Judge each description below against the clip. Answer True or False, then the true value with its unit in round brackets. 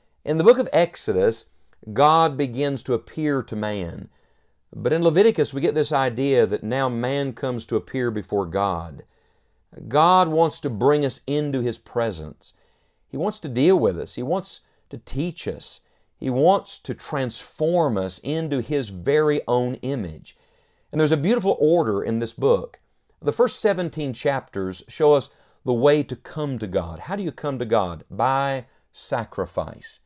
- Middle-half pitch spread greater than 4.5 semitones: True (4.9 semitones)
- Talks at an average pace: True (165 wpm)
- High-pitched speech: False (140 Hz)